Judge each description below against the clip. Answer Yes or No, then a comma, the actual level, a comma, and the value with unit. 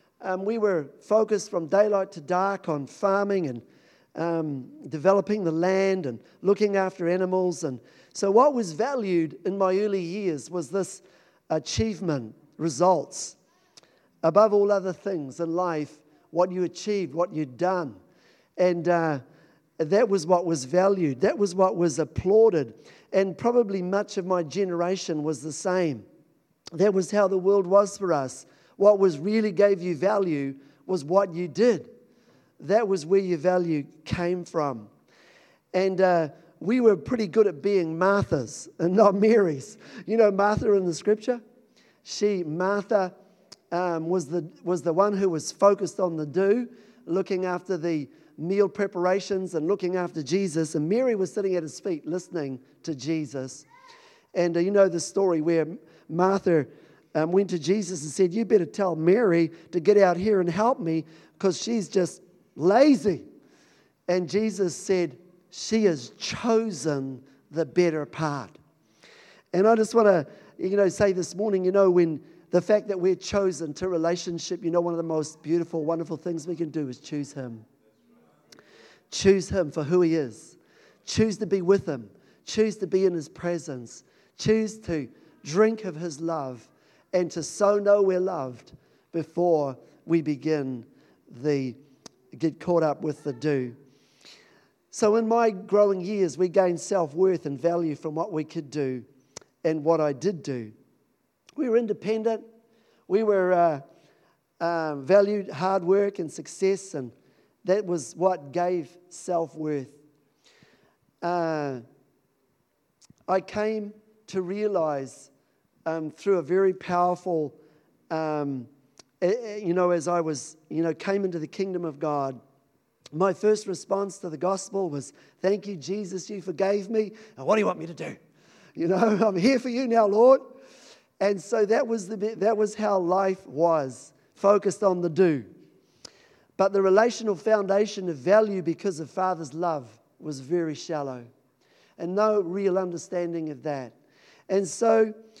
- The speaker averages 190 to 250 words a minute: No, average, 155 wpm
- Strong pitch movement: No, average, 3.9 semitones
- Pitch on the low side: No, medium, 180 Hz